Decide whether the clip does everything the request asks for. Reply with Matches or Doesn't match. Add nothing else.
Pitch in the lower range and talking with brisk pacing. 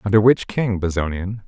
Doesn't match